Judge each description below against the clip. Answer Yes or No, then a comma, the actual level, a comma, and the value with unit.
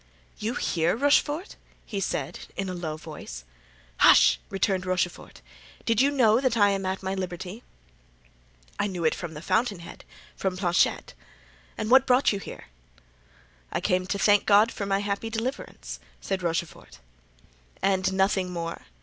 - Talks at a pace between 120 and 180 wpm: Yes, average, 150 wpm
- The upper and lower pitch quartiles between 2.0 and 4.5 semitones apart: Yes, average, 3.5 semitones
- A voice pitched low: No, high, 190 Hz